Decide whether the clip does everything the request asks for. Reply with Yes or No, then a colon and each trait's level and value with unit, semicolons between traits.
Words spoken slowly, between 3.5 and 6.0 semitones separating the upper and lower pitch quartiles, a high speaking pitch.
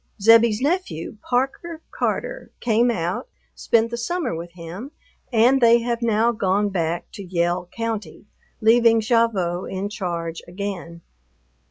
Yes: slow, 130 wpm; average, 4.9 semitones; high, 215 Hz